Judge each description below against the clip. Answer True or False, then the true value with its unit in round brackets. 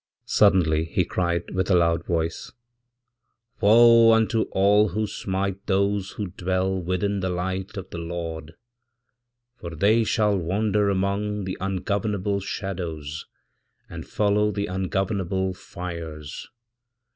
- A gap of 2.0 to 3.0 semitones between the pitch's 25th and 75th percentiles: True (2.7 semitones)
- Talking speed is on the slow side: True (110 wpm)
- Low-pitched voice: True (95 Hz)